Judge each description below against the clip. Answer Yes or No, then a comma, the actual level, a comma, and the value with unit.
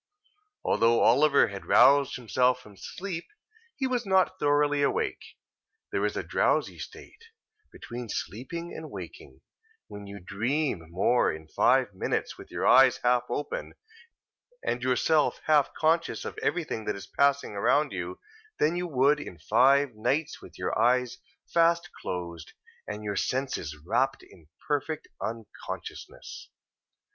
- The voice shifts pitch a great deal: Yes, wide, 6.2 semitones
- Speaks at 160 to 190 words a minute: No, slow, 135 wpm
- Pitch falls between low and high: No, low, 130 Hz